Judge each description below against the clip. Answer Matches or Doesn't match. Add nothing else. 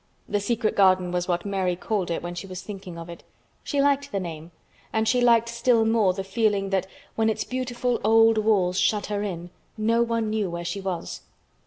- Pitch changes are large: Doesn't match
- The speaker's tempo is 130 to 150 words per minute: Doesn't match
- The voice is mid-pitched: Doesn't match